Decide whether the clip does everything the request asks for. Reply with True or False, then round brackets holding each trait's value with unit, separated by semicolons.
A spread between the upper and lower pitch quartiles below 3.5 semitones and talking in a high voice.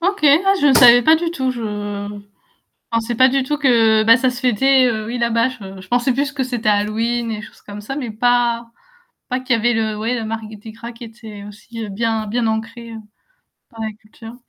True (2.5 semitones; 235 Hz)